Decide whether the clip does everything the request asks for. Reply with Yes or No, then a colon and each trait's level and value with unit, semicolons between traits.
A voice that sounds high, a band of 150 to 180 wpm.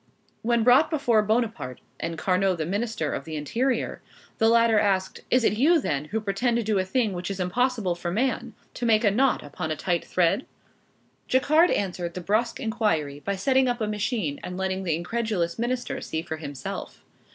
No: high, 210 Hz; average, 190 wpm